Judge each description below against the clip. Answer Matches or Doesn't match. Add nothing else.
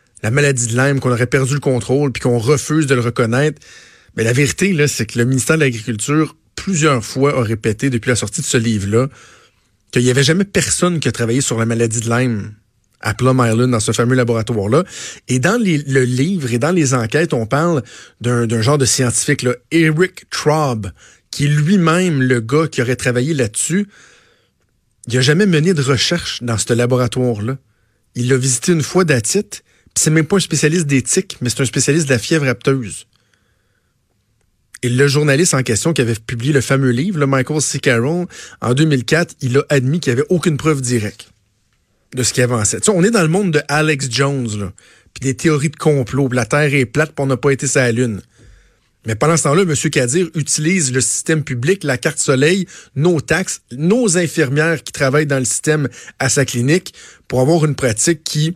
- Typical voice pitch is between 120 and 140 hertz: Matches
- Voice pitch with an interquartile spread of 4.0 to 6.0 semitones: Matches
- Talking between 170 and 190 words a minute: Doesn't match